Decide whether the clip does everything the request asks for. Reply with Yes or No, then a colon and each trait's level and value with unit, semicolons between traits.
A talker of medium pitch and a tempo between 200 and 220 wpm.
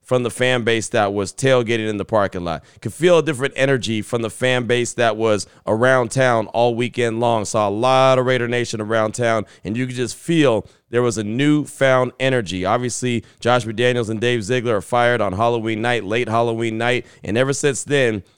No: low, 120 Hz; fast, 205 wpm